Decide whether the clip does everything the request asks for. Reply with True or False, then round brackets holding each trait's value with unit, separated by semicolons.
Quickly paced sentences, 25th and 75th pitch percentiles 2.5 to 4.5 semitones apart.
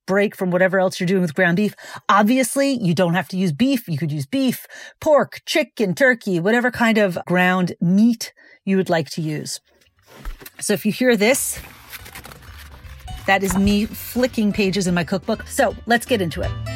False (185 wpm; 3.9 semitones)